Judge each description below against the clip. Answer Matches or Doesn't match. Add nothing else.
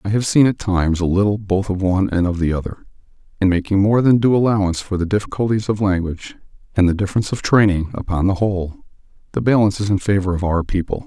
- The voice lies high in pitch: Doesn't match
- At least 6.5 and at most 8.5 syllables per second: Matches